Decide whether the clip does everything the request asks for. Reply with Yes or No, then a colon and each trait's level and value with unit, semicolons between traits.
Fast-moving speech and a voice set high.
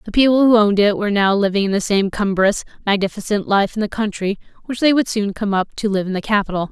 Yes: fast, 240 wpm; high, 205 Hz